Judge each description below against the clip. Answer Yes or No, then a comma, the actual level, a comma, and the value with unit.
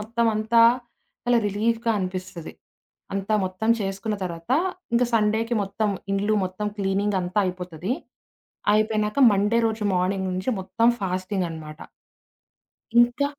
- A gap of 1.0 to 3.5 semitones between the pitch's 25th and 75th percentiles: Yes, average, 3.0 semitones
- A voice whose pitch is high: Yes, high, 200 Hz